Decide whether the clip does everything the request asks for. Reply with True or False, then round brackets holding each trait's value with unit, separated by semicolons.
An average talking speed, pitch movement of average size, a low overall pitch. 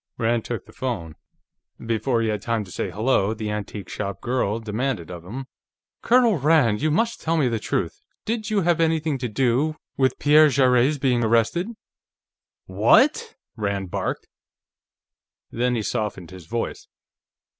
False (155 wpm; 6.1 semitones; 120 Hz)